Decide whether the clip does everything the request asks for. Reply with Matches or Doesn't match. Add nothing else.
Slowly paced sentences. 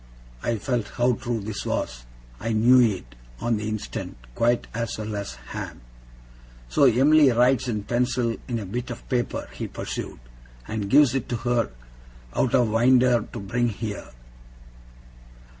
Doesn't match